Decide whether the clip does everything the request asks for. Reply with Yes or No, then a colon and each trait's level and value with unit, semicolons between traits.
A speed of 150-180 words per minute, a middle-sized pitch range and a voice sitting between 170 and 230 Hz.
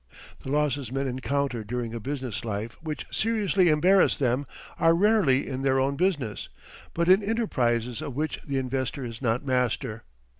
No: average, 160 wpm; average, 4.1 semitones; low, 135 Hz